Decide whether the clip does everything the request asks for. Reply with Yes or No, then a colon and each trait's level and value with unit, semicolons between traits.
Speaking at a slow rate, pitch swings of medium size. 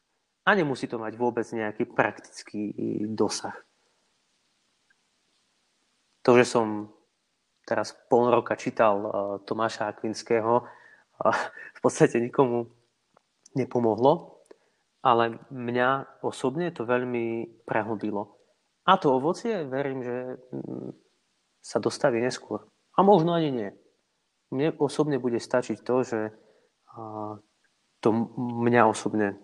Yes: slow, 100 wpm; average, 3.0 semitones